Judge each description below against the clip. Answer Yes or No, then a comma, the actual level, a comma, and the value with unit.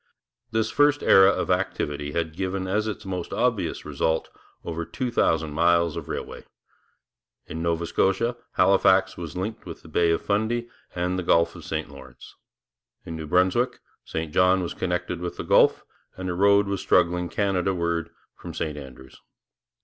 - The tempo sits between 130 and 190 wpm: Yes, average, 165 wpm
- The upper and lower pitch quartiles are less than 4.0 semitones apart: Yes, average, 2.9 semitones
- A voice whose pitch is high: No, very low, 90 Hz